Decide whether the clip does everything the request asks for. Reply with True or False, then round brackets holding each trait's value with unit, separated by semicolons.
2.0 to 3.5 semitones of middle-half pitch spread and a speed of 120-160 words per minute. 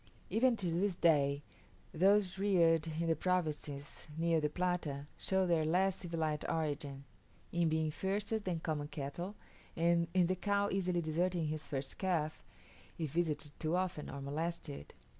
True (3.1 semitones; 150 wpm)